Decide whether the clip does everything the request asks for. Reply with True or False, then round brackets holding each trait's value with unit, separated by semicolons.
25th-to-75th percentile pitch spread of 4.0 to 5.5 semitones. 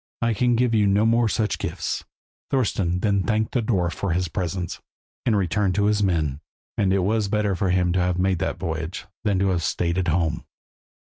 False (3.2 semitones)